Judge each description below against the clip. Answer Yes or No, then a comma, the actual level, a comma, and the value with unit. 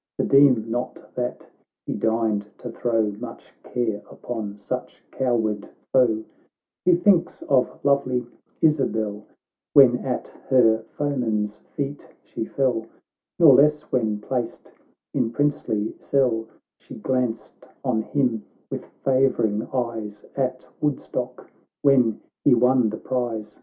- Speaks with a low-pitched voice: Yes, low, 120 Hz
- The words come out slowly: Yes, slow, 125 wpm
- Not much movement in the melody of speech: No, average, 3.2 semitones